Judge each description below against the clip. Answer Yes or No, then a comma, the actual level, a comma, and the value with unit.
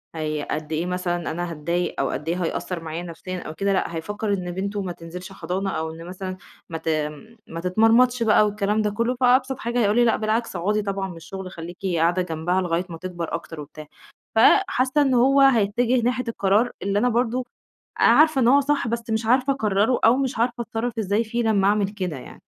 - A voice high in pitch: Yes, high, 200 Hz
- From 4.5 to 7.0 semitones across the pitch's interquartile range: Yes, average, 5.1 semitones